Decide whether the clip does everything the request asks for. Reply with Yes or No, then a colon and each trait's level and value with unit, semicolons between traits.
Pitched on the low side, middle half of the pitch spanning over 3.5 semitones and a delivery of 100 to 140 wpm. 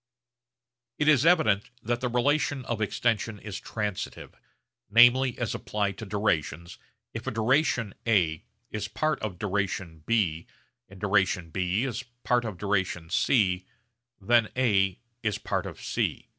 Yes: low, 105 Hz; average, 4.0 semitones; slow, 135 wpm